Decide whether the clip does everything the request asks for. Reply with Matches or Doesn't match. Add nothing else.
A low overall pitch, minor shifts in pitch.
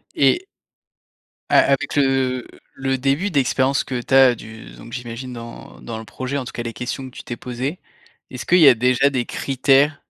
Matches